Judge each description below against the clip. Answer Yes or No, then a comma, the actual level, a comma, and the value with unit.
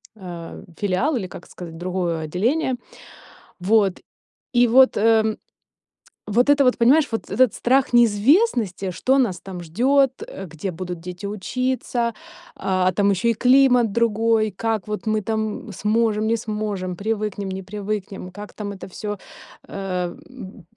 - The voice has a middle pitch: No, high, 210 Hz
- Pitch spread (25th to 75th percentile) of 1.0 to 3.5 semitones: No, average, 3.9 semitones